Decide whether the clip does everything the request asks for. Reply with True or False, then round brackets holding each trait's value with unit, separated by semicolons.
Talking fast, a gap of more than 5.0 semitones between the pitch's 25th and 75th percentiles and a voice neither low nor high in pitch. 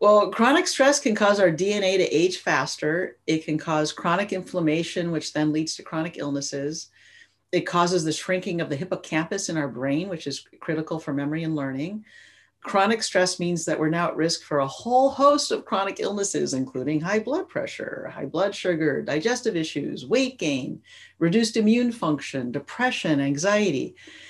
False (170 wpm; 5.5 semitones; 175 Hz)